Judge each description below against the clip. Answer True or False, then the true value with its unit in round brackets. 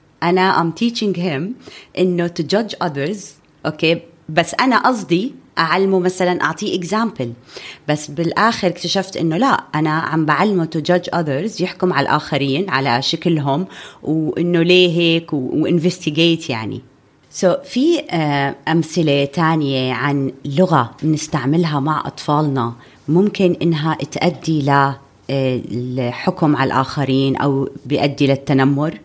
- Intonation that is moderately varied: True (4.3 semitones)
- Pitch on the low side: False (160 Hz)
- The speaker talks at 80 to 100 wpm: False (120 wpm)